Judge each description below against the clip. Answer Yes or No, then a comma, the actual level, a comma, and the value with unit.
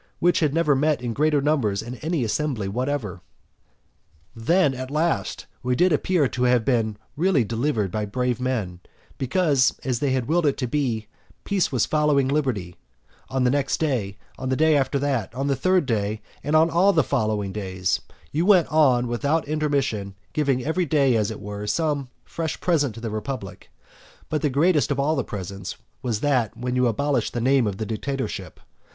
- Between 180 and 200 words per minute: Yes, average, 185 wpm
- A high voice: No, low, 130 Hz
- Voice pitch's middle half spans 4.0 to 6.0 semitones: Yes, average, 5.0 semitones